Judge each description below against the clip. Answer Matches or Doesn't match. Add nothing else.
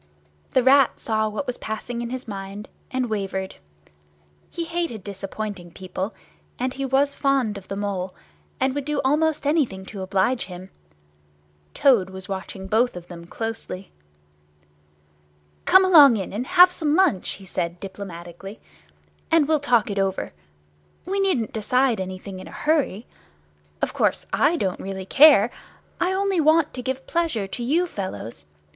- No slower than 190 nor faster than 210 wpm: Doesn't match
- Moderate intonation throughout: Doesn't match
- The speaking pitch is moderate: Doesn't match